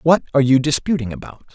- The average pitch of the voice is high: No, medium, 140 Hz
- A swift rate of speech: No, average, 195 wpm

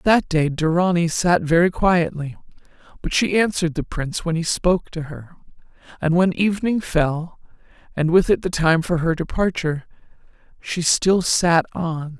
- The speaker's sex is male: No, female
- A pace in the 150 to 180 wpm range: Yes, average, 155 wpm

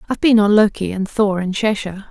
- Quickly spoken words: Yes, fast, 230 wpm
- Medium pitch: No, high, 205 Hz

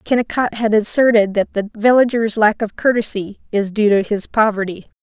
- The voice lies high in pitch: Yes, high, 215 Hz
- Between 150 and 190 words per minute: Yes, average, 165 wpm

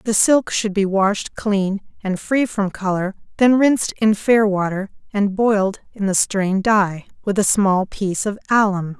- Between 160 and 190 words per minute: Yes, average, 180 wpm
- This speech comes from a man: No, female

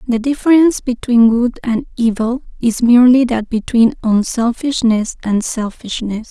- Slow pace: Yes, slow, 125 wpm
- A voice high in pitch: Yes, high, 235 Hz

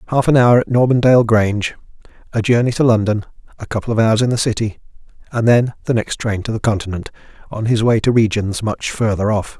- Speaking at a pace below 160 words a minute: No, average, 190 wpm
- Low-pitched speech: Yes, low, 115 Hz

